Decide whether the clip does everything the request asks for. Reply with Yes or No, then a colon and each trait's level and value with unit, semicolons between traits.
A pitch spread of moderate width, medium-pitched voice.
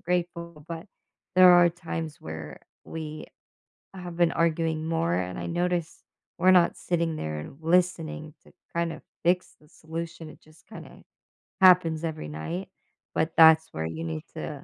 No: narrow, 2.2 semitones; medium, 165 Hz